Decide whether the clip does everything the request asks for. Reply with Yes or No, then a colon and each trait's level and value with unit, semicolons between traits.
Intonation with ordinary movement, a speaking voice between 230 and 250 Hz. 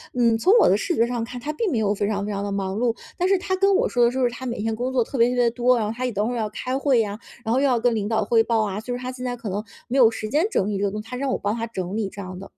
Yes: average, 3.2 semitones; high, 235 Hz